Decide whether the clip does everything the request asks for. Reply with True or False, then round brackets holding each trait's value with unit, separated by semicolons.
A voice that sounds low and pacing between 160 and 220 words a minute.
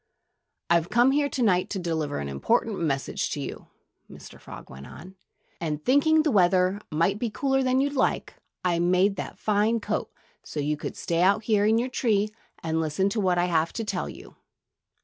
False (195 Hz; 200 wpm)